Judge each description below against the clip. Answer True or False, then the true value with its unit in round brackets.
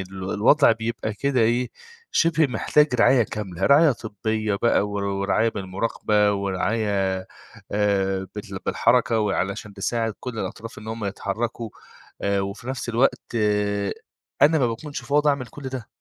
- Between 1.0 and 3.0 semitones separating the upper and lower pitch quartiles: False (3.7 semitones)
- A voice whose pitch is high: False (110 Hz)